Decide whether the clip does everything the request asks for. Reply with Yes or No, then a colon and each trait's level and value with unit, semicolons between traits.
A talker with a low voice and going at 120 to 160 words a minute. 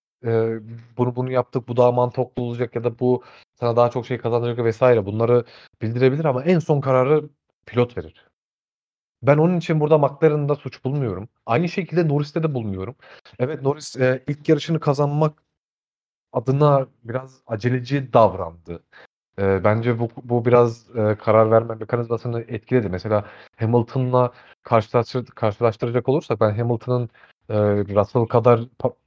Yes: low, 125 Hz; fast, 140 wpm